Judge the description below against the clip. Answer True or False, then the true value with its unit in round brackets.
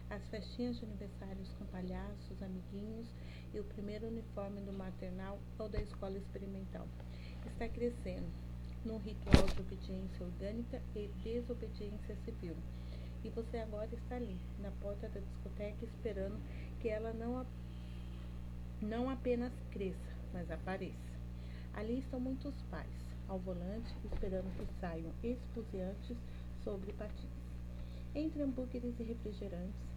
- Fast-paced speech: False (125 wpm)